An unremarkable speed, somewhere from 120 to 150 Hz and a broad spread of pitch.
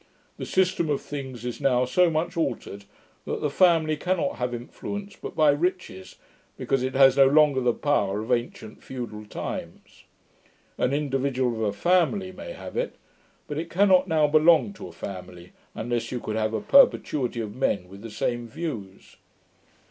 Yes: average, 170 wpm; low, 135 Hz; wide, 6.4 semitones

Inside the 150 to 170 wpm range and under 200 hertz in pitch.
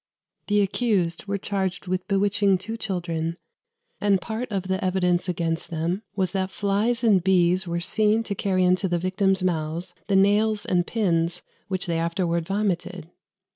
Yes: average, 160 wpm; high, 190 Hz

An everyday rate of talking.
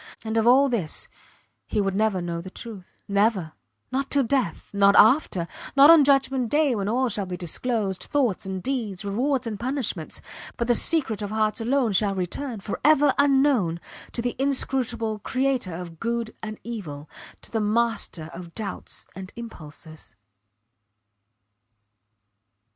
Yes: average, 150 wpm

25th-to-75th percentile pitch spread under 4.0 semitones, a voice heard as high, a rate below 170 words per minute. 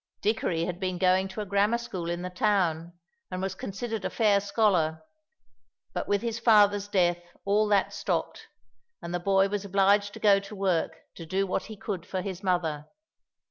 No: narrow, 2.4 semitones; high, 195 Hz; average, 185 wpm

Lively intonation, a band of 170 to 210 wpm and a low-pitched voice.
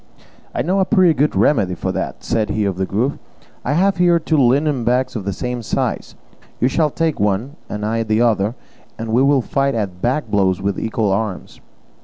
Yes: wide, 5.8 semitones; average, 200 wpm; low, 120 Hz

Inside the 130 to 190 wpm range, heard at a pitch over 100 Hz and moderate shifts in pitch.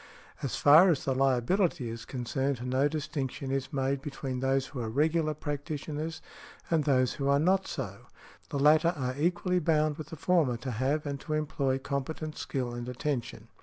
Yes: average, 180 wpm; medium, 140 Hz; average, 3.0 semitones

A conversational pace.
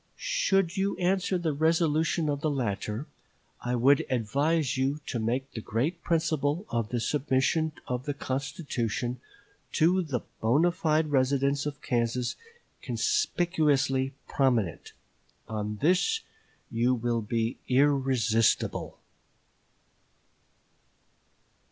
No: slow, 105 wpm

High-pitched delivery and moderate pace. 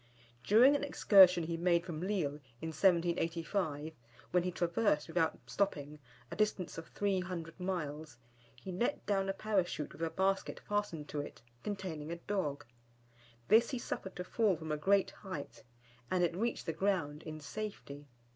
No: medium, 175 Hz; average, 160 wpm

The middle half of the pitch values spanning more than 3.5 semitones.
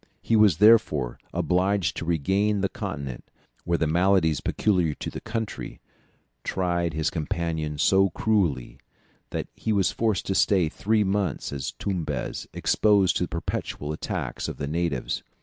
Yes: average, 4.4 semitones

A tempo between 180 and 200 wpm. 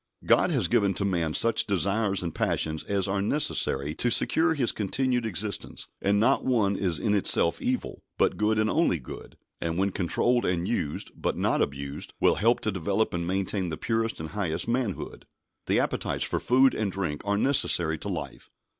Yes: average, 185 wpm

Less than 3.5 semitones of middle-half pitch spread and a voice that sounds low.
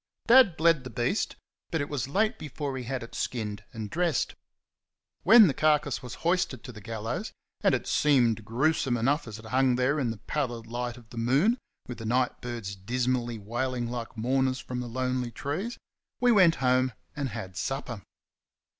No: average, 3.8 semitones; low, 125 Hz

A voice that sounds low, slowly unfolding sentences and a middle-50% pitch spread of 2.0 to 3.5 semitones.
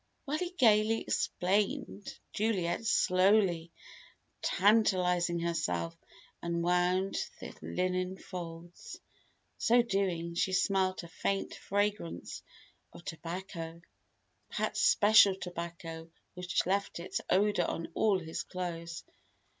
No: medium, 185 Hz; slow, 100 wpm; average, 3.0 semitones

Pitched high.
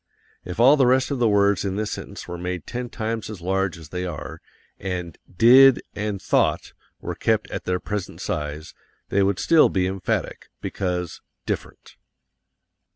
No: very low, 95 Hz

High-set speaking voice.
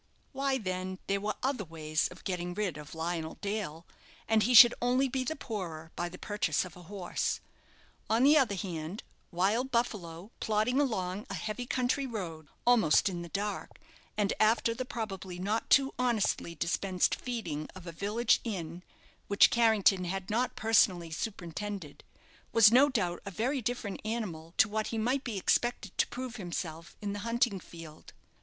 Yes: high, 205 Hz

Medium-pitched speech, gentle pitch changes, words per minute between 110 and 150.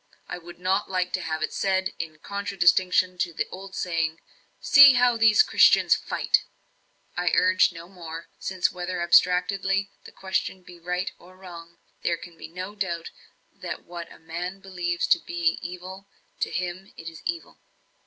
No: medium, 180 Hz; narrow, 1.9 semitones; average, 165 wpm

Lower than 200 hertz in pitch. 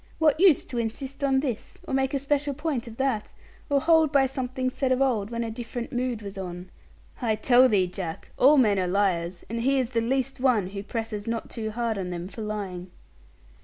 No: high, 235 Hz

